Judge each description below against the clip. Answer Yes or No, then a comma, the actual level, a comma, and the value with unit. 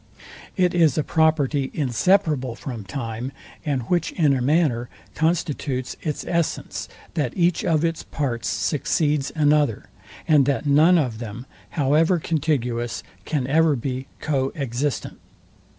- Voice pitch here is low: No, medium, 145 Hz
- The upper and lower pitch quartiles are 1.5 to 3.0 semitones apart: No, average, 3.8 semitones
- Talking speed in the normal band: No, slow, 130 wpm